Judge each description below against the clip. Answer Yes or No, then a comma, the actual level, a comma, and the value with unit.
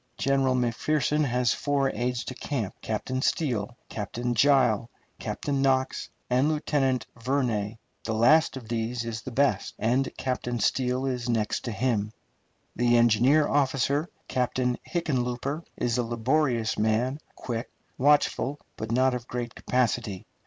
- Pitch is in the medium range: No, low, 125 Hz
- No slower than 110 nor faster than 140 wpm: Yes, slow, 135 wpm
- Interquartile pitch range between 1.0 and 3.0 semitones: Yes, narrow, 2.6 semitones